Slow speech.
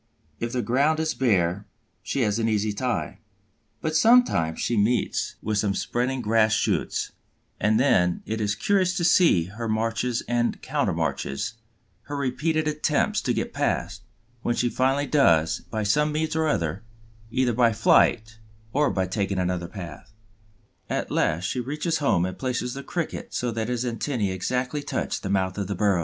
No: average, 170 wpm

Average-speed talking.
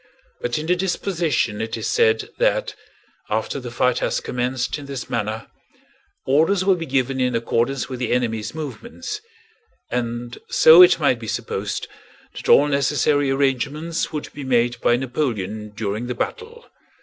Yes: average, 155 wpm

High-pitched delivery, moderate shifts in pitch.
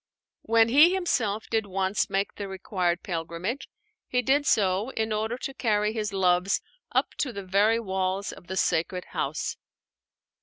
Yes: high, 205 Hz; average, 3.3 semitones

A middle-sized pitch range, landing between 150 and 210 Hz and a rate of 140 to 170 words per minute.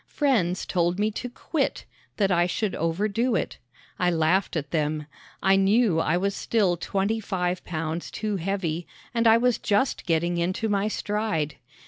Yes: average, 4.0 semitones; high, 190 Hz; average, 160 wpm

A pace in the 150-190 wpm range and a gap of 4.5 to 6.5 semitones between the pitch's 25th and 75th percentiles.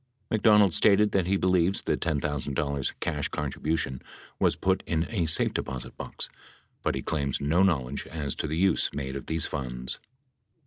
Yes: average, 165 wpm; average, 4.8 semitones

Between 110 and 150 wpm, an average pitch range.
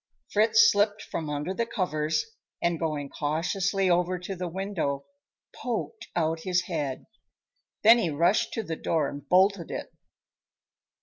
Yes: average, 140 wpm; average, 4.0 semitones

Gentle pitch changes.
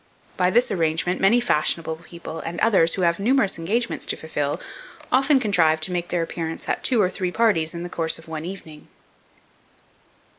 No: average, 3.9 semitones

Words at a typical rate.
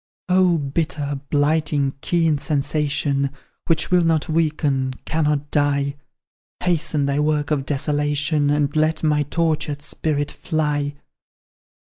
No: slow, 110 wpm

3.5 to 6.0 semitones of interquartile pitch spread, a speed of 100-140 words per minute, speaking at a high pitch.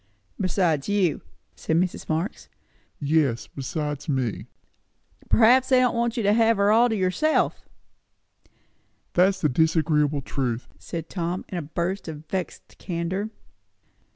No: average, 5.2 semitones; slow, 135 wpm; medium, 175 Hz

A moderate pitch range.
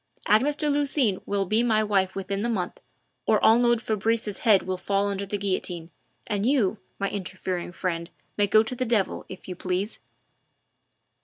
Yes: average, 3.2 semitones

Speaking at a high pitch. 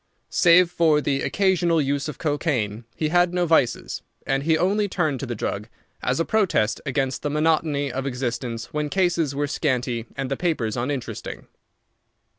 No: medium, 145 Hz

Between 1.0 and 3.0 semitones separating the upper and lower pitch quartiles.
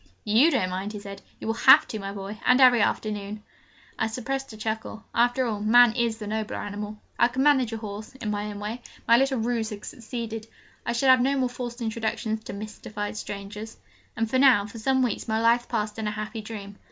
Yes: narrow, 2.5 semitones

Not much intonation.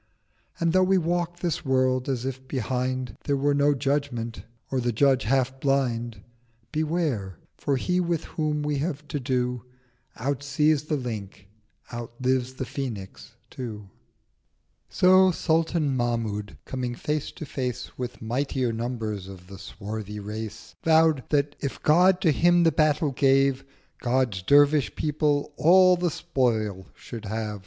No: average, 4.3 semitones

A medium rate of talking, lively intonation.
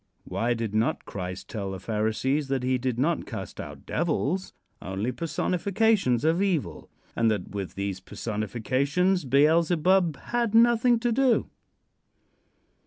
No: slow, 130 wpm; wide, 8.7 semitones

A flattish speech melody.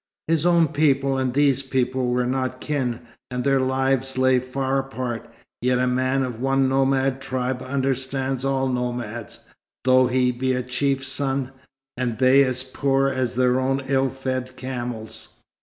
Yes: narrow, 1.1 semitones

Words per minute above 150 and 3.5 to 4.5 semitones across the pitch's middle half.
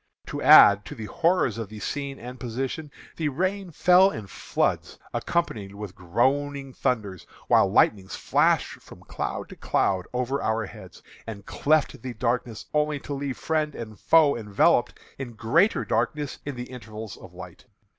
No: average, 160 wpm; average, 5.3 semitones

